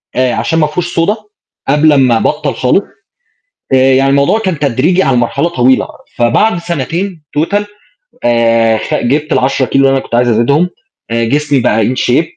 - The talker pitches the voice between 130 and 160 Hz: Yes, low, 135 Hz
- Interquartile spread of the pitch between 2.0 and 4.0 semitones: No, average, 5.1 semitones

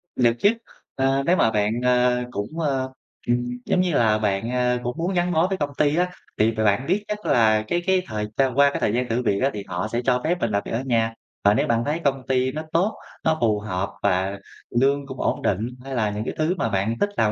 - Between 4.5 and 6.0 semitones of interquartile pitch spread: Yes, average, 5.1 semitones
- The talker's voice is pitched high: No, low, 125 Hz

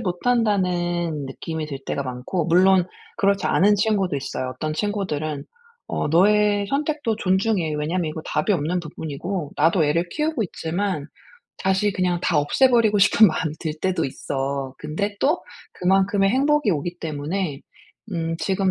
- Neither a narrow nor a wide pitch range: Yes, average, 4.7 semitones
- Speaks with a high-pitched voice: No, medium, 180 Hz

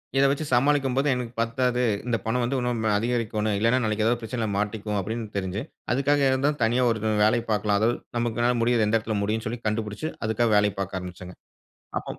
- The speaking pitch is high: No, low, 115 Hz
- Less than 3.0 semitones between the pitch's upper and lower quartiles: Yes, narrow, 2.5 semitones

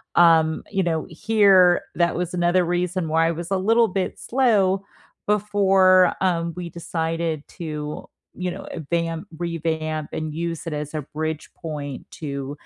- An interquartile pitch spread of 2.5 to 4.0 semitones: Yes, average, 2.8 semitones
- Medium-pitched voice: Yes, medium, 170 Hz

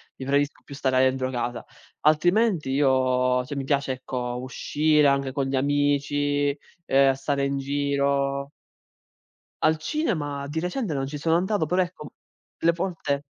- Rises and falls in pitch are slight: Yes, narrow, 2.2 semitones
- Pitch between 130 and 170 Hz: Yes, medium, 140 Hz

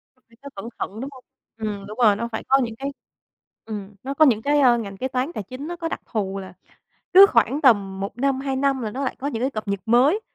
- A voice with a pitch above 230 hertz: Yes, high, 240 Hz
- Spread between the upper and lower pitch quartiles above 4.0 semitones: Yes, average, 4.5 semitones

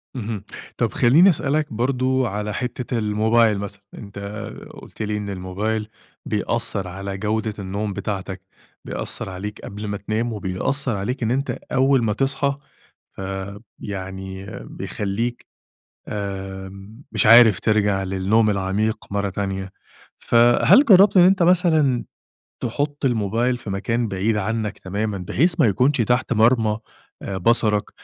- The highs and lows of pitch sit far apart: No, average, 3.8 semitones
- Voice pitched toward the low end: Yes, low, 110 Hz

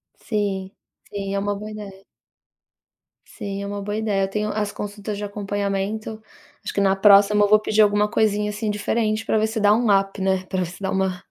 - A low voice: No, high, 205 Hz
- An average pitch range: No, narrow, 1.4 semitones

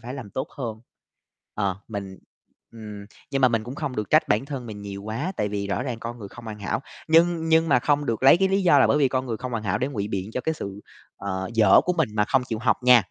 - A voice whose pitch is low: Yes, low, 115 Hz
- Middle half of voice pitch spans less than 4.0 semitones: No, average, 4.9 semitones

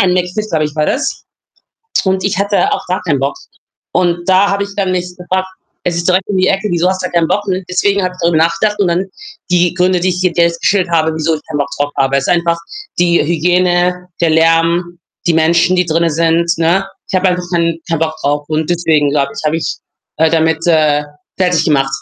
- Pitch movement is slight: Yes, narrow, 2.2 semitones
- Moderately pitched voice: Yes, medium, 175 Hz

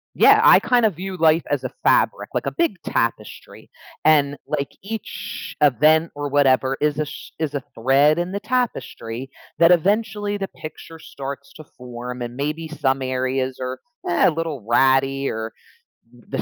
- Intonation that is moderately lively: Yes, average, 4.4 semitones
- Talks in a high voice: No, medium, 145 Hz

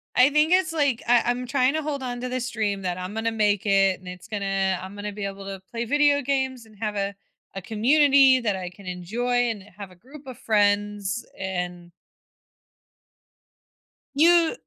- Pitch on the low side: No, high, 220 Hz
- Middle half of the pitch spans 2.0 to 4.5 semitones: No, average, 4.9 semitones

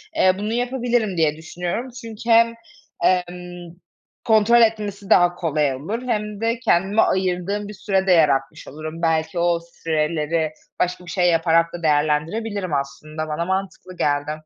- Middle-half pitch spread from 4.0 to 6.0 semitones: Yes, average, 4.7 semitones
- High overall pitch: No, medium, 180 Hz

